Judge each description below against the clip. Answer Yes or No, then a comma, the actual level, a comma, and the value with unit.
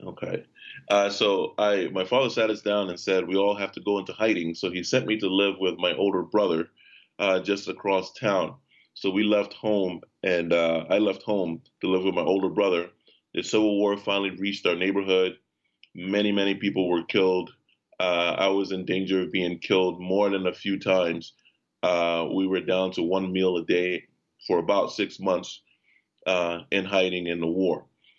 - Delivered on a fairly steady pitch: Yes, narrow, 1.8 semitones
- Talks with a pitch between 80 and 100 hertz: Yes, very low, 95 Hz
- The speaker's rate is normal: Yes, average, 195 wpm